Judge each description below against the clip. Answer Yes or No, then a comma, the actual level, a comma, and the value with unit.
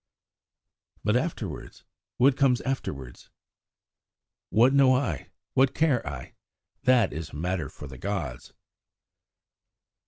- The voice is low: Yes, low, 110 Hz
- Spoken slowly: Yes, slow, 105 wpm